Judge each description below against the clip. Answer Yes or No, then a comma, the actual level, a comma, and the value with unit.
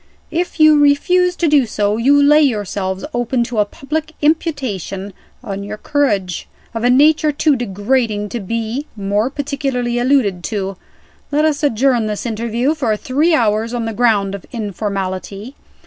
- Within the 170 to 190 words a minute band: No, average, 155 wpm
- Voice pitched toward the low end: No, high, 240 Hz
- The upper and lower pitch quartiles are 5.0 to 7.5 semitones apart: Yes, wide, 5.6 semitones